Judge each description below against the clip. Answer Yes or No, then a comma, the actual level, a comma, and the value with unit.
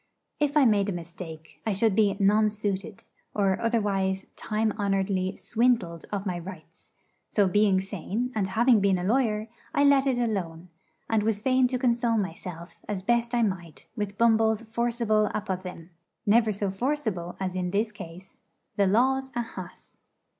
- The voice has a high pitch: Yes, high, 205 Hz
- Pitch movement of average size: Yes, average, 3.5 semitones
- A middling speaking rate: Yes, average, 160 wpm